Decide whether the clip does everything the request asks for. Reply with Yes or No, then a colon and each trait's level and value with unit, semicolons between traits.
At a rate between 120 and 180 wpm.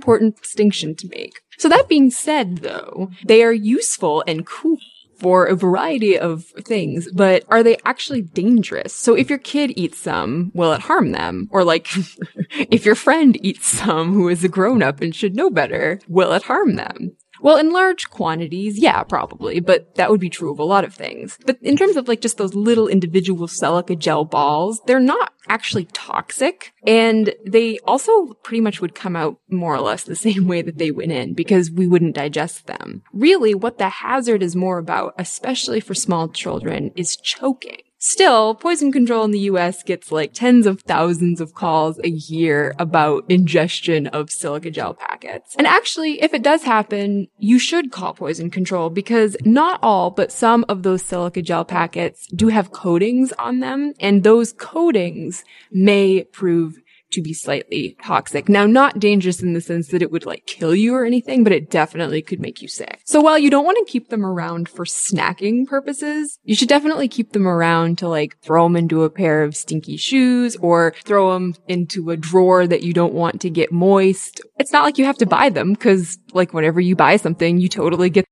No: average, 195 wpm